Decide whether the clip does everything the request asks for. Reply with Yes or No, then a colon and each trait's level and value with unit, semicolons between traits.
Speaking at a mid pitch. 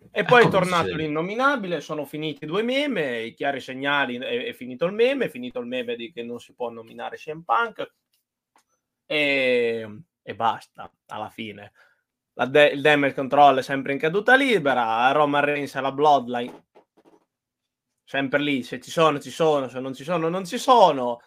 Yes: medium, 145 Hz